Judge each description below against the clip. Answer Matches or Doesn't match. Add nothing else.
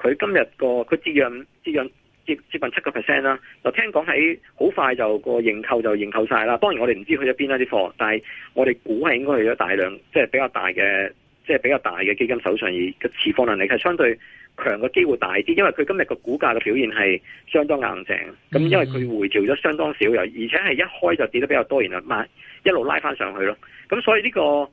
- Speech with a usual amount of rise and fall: Doesn't match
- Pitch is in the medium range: Doesn't match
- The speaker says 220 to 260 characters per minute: Doesn't match